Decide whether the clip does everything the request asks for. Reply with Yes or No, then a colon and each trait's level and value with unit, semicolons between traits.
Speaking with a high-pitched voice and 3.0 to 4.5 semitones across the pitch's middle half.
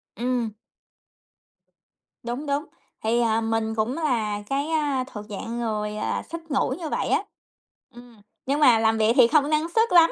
No: high, 240 Hz; average, 4.9 semitones